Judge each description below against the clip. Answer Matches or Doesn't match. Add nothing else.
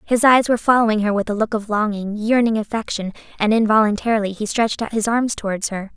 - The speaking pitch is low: Doesn't match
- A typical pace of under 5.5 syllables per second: Doesn't match